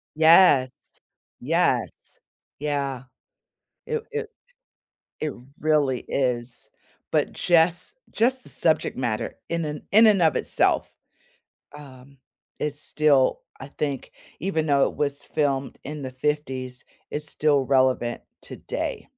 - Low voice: No, medium, 145 Hz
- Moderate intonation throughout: Yes, average, 3.2 semitones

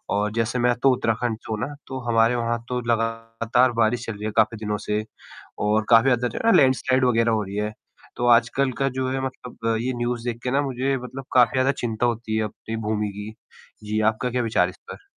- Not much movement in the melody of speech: Yes, narrow, 2.3 semitones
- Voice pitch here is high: No, low, 115 Hz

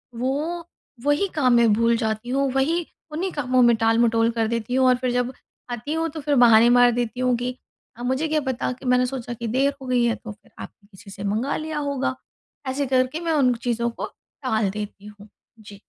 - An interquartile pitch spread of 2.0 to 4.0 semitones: Yes, average, 2.9 semitones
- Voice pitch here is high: Yes, high, 245 Hz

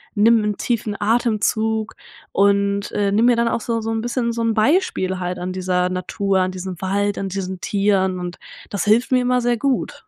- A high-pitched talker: Yes, high, 205 Hz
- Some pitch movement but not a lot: Yes, average, 3.5 semitones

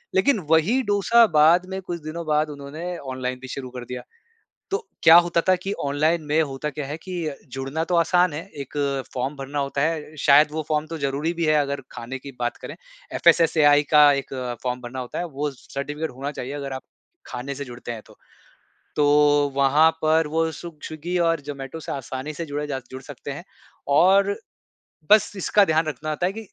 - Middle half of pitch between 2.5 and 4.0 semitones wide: Yes, average, 3.1 semitones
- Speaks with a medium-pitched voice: Yes, medium, 150 Hz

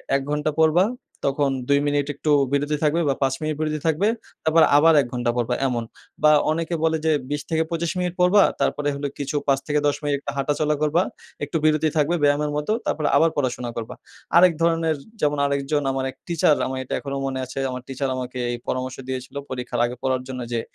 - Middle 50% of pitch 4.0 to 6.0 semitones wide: No, average, 2.8 semitones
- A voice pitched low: No, medium, 145 Hz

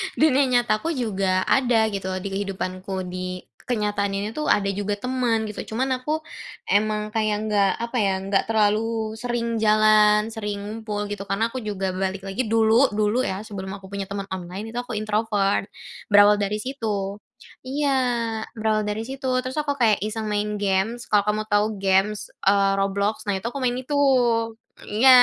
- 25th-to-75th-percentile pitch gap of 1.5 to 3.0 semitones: Yes, narrow, 2.6 semitones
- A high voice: Yes, high, 210 Hz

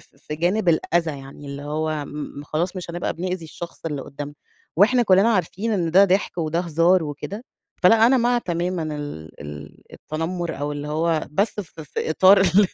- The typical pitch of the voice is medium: Yes, medium, 170 Hz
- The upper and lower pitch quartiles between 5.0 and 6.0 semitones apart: No, average, 3.8 semitones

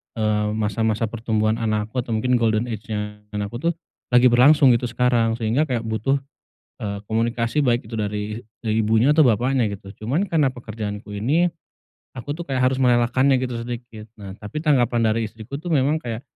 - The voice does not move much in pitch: No, average, 3.0 semitones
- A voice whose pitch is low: Yes, low, 115 Hz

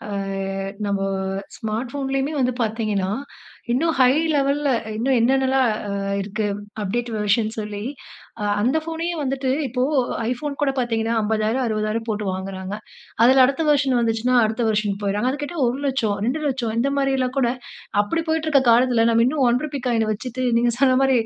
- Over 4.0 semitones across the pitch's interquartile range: No, average, 3.7 semitones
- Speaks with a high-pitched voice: Yes, high, 245 Hz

